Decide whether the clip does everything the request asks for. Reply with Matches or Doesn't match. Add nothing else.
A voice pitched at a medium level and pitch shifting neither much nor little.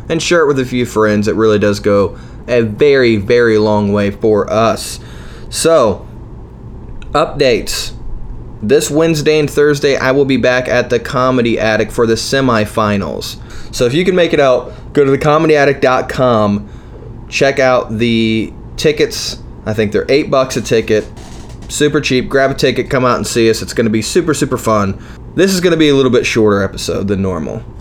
Doesn't match